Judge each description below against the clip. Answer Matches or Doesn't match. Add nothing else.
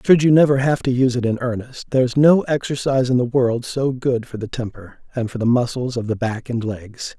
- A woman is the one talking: Doesn't match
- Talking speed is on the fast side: Matches